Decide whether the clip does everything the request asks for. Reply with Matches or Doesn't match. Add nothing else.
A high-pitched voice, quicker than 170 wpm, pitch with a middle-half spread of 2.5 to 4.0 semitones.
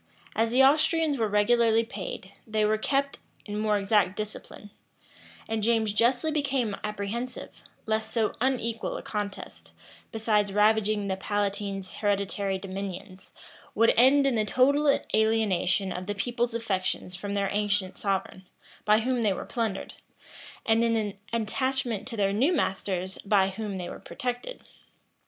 Doesn't match